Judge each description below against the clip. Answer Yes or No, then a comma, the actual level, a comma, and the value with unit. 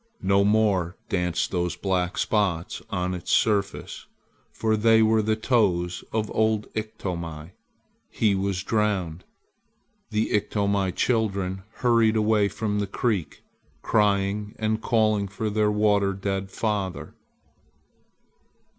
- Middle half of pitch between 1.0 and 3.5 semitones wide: Yes, narrow, 2.4 semitones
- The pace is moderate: No, slow, 115 wpm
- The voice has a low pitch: Yes, low, 105 Hz